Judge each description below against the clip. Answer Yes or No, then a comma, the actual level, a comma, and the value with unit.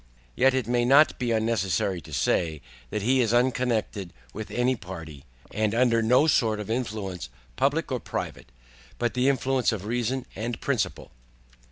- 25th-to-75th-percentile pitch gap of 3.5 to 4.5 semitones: Yes, average, 3.8 semitones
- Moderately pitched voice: No, low, 115 Hz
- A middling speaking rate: Yes, average, 160 wpm